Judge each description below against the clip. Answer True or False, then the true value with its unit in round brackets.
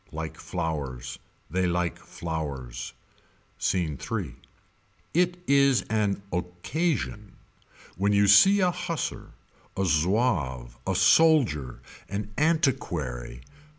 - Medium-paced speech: False (95 wpm)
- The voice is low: True (90 Hz)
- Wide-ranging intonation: True (8.9 semitones)